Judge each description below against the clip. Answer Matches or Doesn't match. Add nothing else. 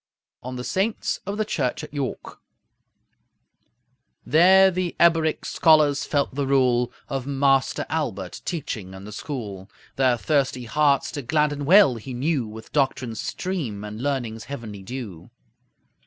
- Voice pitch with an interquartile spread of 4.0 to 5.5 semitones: Matches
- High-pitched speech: Doesn't match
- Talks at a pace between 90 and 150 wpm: Matches